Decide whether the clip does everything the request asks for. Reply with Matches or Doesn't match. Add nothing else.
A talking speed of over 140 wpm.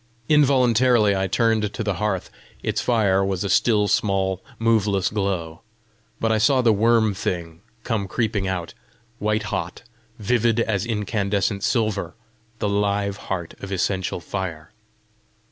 Doesn't match